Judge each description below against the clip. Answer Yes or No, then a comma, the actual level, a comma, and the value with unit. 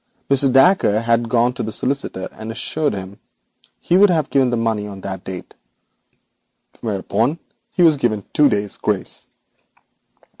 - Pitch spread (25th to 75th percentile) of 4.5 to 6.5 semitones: Yes, average, 5.2 semitones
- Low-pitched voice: Yes, low, 115 Hz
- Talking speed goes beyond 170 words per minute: No, average, 145 wpm